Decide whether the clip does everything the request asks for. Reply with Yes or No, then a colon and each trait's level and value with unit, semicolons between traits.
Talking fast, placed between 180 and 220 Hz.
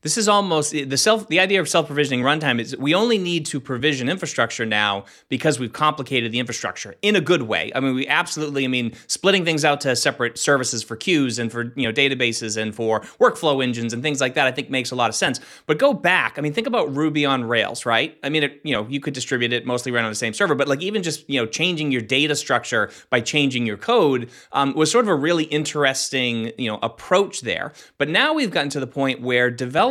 No: fast, 245 wpm; low, 135 Hz